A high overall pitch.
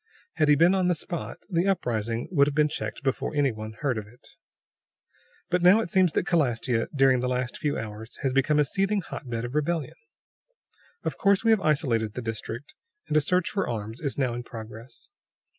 No: medium, 140 Hz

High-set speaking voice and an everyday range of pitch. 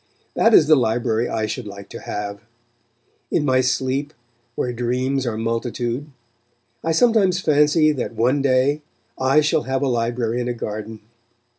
No: low, 130 Hz; average, 3.9 semitones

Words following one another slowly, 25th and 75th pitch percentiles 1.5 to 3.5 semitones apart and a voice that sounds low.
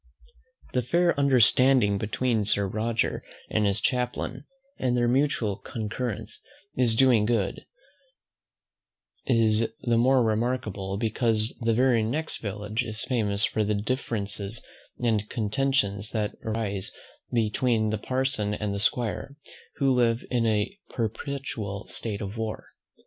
Yes: slow, 125 wpm; average, 3.1 semitones; low, 115 Hz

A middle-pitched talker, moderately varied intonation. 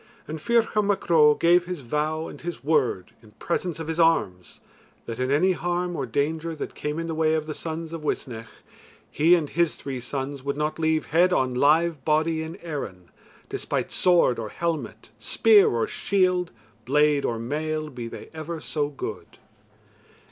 Yes: medium, 155 Hz; average, 3.2 semitones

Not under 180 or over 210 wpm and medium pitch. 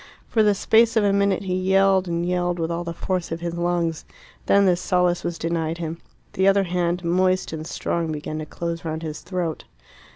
Yes: fast, 205 wpm; medium, 175 Hz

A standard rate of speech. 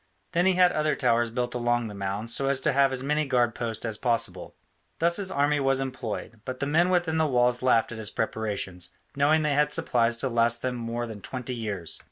No: fast, 225 wpm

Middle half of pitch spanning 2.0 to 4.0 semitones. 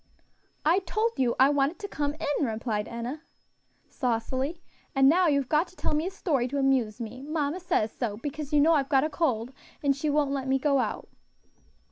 Yes: average, 3.2 semitones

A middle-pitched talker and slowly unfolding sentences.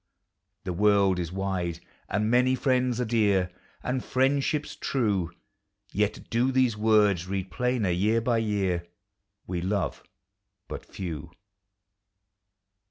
No: low, 105 Hz; slow, 115 wpm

